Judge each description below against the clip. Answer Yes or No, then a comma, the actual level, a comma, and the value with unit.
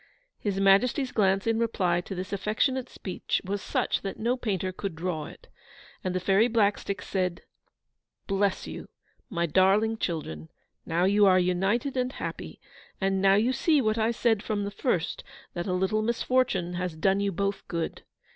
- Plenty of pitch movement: No, average, 3.3 semitones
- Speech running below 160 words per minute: No, average, 170 wpm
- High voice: Yes, high, 195 Hz